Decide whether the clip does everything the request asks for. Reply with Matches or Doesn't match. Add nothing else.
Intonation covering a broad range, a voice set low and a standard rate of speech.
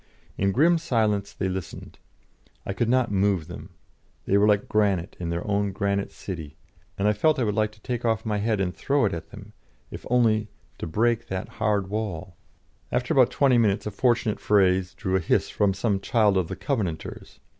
Doesn't match